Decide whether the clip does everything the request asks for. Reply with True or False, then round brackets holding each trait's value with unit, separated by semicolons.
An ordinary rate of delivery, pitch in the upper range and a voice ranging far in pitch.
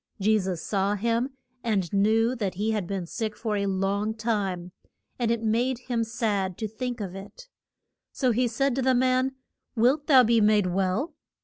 False (185 wpm; 220 Hz; 3.6 semitones)